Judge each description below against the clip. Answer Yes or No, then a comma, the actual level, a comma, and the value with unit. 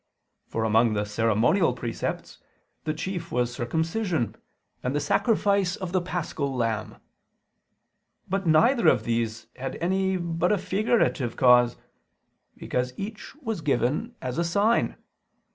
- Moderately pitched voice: Yes, medium, 160 Hz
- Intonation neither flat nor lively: No, wide, 7.9 semitones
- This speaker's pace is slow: Yes, slow, 125 wpm